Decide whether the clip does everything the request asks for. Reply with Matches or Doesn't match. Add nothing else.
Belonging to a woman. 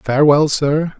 Doesn't match